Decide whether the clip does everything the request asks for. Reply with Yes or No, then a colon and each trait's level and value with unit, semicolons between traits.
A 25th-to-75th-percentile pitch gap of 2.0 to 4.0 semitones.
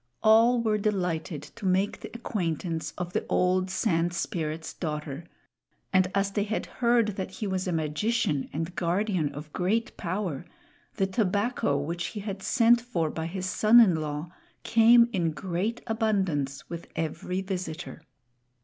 No: average, 4.6 semitones